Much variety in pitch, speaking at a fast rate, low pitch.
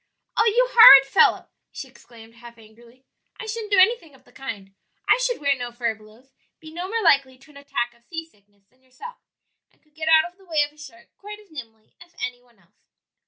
No: wide, 6.8 semitones; fast, 220 wpm; very high, 275 Hz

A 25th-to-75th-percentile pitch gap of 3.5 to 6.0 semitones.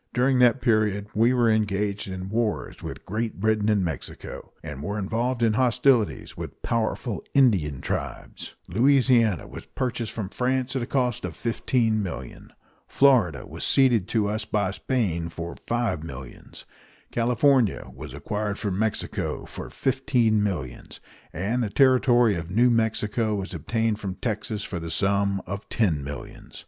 Yes: average, 3.8 semitones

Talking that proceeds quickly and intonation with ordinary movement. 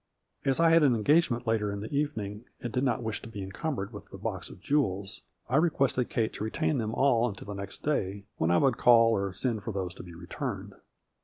Yes: fast, 230 wpm; average, 4.9 semitones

